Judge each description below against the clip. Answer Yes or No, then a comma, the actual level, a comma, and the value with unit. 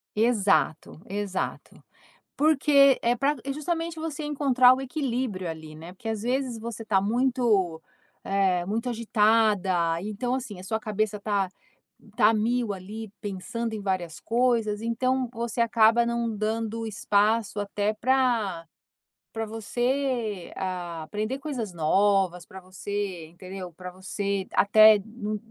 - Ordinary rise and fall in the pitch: Yes, average, 3.8 semitones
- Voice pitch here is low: No, high, 215 Hz